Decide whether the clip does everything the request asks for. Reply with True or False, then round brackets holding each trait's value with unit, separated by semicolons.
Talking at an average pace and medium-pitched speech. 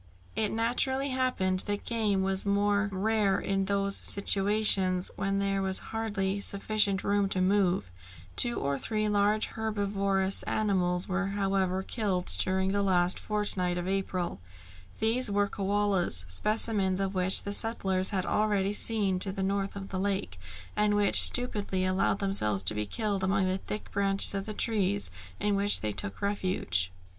False (155 wpm; 195 Hz)